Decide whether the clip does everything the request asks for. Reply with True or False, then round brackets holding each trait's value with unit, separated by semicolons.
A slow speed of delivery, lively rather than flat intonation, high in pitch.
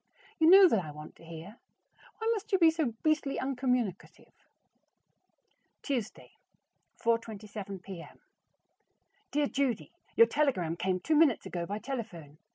True (130 wpm; 8.0 semitones; 230 Hz)